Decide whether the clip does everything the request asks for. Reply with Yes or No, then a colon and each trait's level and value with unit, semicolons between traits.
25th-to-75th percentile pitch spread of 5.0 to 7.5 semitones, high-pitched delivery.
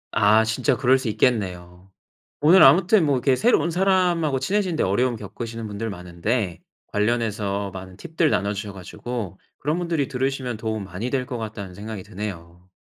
No: wide, 5.5 semitones; low, 115 Hz